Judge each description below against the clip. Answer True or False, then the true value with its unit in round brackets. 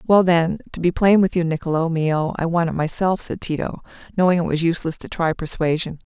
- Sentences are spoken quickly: True (215 wpm)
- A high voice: False (165 Hz)